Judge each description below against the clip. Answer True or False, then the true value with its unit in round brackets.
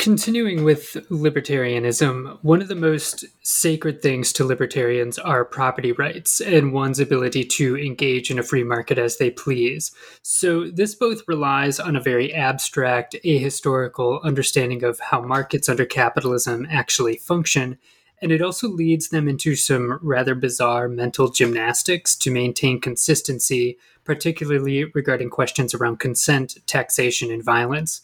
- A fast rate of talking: False (140 wpm)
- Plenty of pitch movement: False (3.8 semitones)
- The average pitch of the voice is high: False (135 Hz)